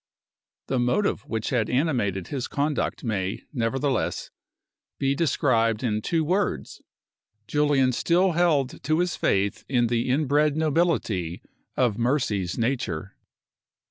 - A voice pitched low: Yes, low, 130 Hz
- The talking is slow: Yes, slow, 115 wpm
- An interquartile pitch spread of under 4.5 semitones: No, average, 5.0 semitones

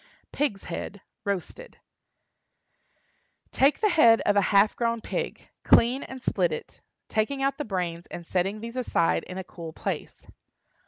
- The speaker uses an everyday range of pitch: No, wide, 6.2 semitones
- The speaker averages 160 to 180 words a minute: No, average, 150 wpm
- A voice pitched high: Yes, high, 220 Hz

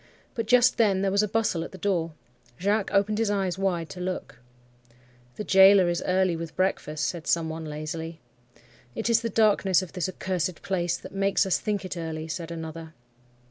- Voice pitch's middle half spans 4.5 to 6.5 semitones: No, average, 3.3 semitones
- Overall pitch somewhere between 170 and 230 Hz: Yes, medium, 185 Hz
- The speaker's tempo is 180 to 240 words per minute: Yes, average, 190 wpm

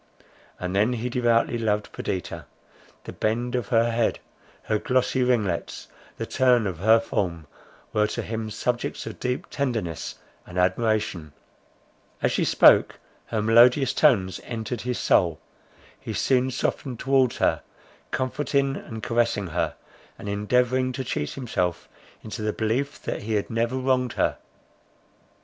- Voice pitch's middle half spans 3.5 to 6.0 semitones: No, average, 3.1 semitones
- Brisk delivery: No, average, 140 wpm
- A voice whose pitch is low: Yes, low, 115 Hz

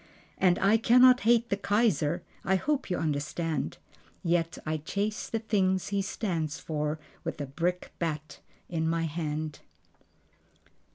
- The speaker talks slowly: Yes, slow, 130 wpm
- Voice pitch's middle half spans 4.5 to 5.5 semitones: Yes, average, 4.8 semitones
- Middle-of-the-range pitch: Yes, medium, 175 Hz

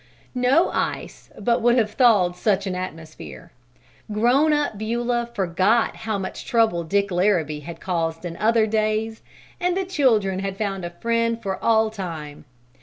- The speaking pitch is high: Yes, high, 210 Hz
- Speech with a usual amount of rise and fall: Yes, average, 4.2 semitones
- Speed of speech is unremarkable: Yes, average, 160 wpm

